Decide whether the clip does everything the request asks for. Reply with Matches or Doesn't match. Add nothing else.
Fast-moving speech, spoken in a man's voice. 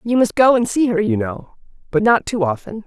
Doesn't match